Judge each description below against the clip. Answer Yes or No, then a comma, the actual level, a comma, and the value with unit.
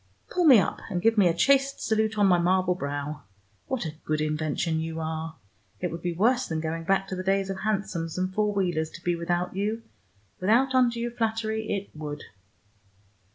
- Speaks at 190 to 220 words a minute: Yes, average, 195 wpm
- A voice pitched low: No, medium, 185 Hz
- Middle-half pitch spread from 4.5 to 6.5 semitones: Yes, average, 5.0 semitones